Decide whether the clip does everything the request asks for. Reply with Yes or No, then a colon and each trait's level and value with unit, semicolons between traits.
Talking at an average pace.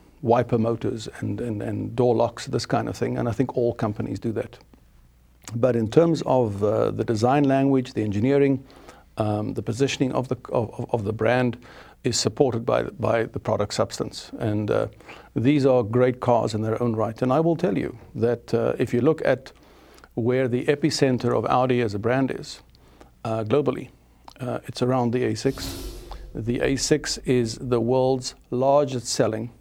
Yes: average, 180 wpm